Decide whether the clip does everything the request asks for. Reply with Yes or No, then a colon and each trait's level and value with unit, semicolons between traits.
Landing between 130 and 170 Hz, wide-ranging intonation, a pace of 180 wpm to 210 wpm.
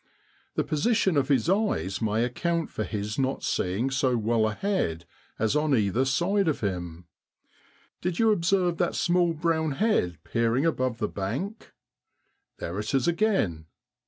No: low, 135 Hz; wide, 8.3 semitones; average, 150 wpm